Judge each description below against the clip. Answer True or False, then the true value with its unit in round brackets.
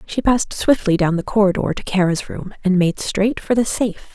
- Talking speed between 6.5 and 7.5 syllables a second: False (5.4 syllables/s)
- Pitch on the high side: True (200 Hz)